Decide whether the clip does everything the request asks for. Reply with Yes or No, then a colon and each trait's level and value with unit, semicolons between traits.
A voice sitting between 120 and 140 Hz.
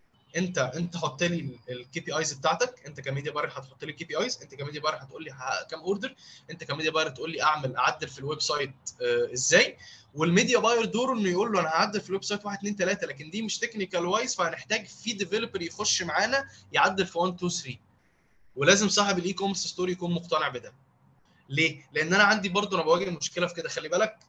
No: medium, 175 Hz